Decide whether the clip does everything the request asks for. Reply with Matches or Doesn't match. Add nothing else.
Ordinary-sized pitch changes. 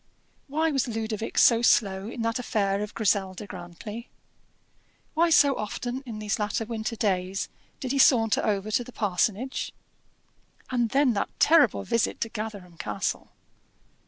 Matches